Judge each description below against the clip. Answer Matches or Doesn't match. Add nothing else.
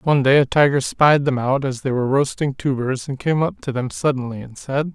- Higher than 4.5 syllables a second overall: Matches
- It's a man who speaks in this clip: Matches